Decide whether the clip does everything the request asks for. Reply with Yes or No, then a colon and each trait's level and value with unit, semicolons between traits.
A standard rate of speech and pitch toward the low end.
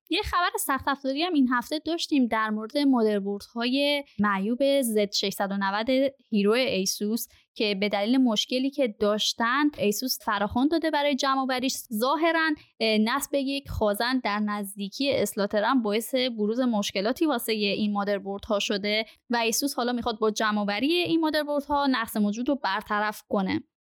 No: average, 145 wpm; high, 235 Hz